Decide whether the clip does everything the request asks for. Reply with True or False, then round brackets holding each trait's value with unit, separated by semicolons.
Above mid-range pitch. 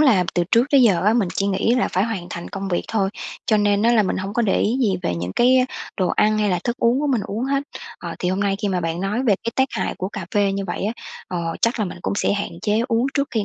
True (205 Hz)